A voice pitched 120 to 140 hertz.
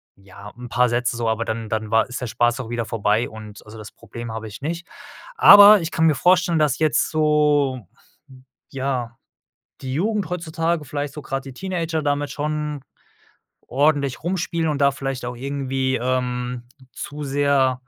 Yes: low, 135 Hz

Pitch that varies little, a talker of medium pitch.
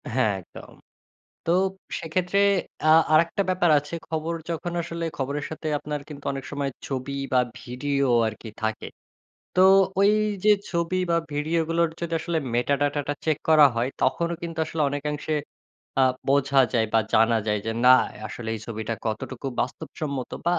No: average, 4.3 semitones; medium, 145 Hz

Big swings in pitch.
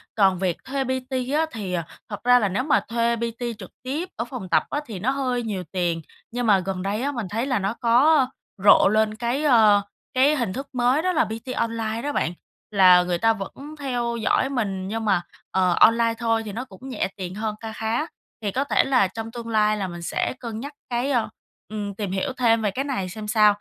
No: average, 4.0 semitones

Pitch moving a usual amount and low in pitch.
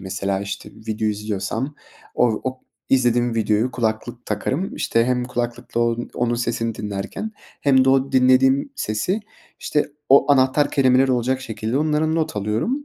Yes: average, 3.3 semitones; low, 120 Hz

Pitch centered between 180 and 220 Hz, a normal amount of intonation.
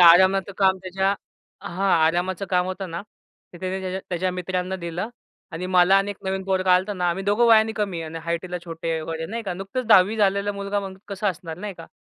No: medium, 185 Hz; narrow, 1.9 semitones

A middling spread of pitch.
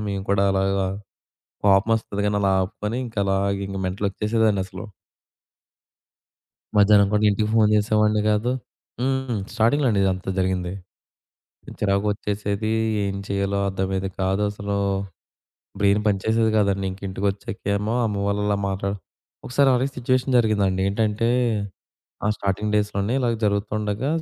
No: narrow, 1.7 semitones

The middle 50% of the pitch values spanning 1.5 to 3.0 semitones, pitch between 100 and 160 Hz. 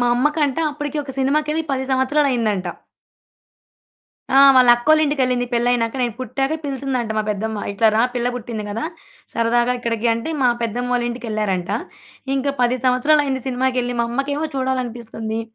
No: average, 2.7 semitones; high, 245 Hz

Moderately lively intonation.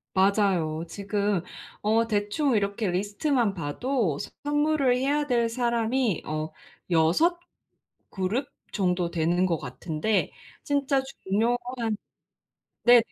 No: wide, 5.8 semitones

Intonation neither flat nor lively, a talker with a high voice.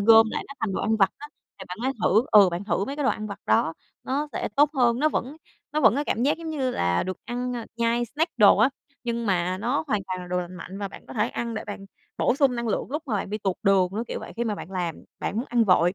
Yes: average, 4.7 semitones; high, 220 Hz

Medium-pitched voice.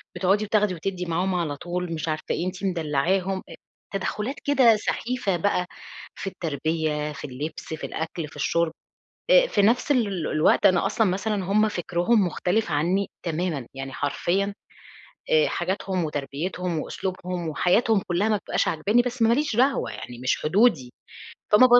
Yes: medium, 180 Hz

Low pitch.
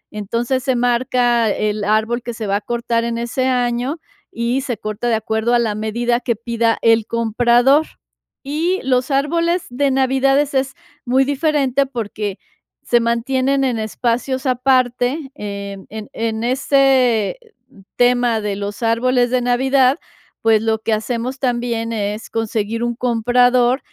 No: high, 240 Hz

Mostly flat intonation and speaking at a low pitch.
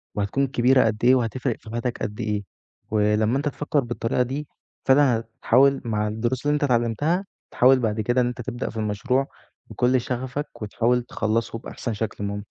No: average, 3.1 semitones; low, 120 Hz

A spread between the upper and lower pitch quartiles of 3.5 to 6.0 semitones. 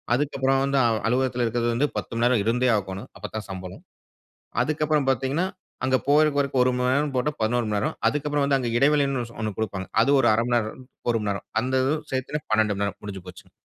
Yes: average, 4.1 semitones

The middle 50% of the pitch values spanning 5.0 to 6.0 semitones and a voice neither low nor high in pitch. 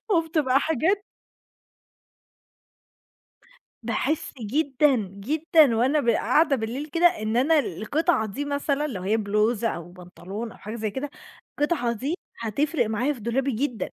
No: wide, 5.4 semitones; very high, 260 Hz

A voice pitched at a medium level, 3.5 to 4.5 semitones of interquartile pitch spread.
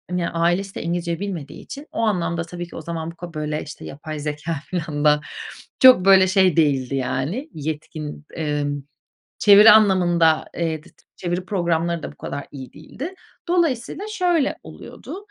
Yes: medium, 170 Hz; average, 4.2 semitones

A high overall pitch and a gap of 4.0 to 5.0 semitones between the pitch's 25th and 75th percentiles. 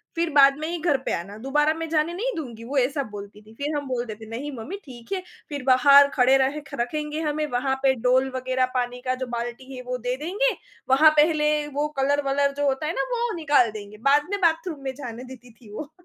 No: very high, 275 Hz; average, 3.5 semitones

